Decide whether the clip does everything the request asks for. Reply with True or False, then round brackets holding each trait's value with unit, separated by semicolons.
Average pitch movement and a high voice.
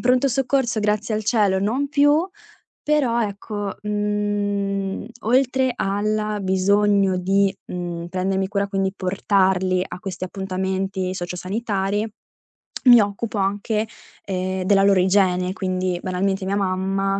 False (2.0 semitones; 200 Hz)